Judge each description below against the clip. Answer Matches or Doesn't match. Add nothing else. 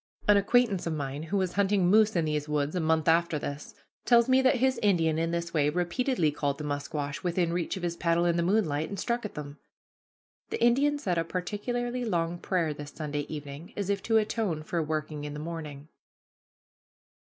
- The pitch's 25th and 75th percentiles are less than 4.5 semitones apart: Doesn't match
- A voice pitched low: Doesn't match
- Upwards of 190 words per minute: Matches